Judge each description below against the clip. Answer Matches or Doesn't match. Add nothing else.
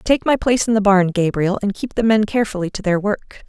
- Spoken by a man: Doesn't match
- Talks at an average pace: Doesn't match